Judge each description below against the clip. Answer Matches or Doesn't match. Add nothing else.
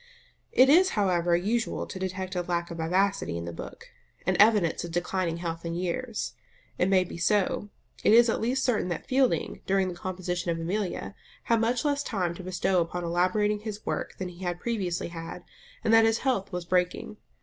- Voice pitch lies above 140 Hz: Matches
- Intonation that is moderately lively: Matches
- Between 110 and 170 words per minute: Doesn't match